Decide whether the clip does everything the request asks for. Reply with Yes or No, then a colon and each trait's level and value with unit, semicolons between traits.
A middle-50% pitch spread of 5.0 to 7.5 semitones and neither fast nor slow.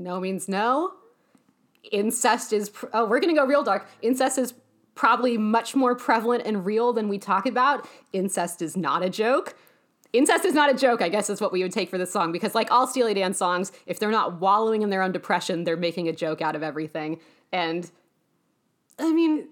No: wide, 5.5 semitones; fast, 210 wpm